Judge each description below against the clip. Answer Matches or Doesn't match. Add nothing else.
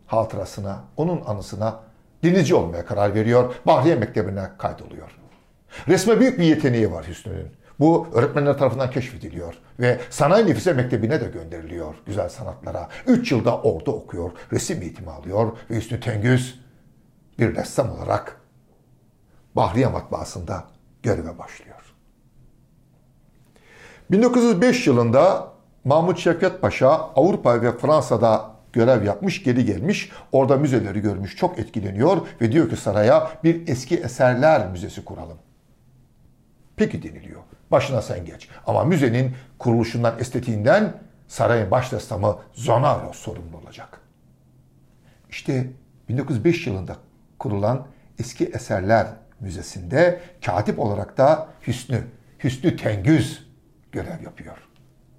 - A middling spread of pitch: Doesn't match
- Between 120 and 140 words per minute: Doesn't match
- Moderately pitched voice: Doesn't match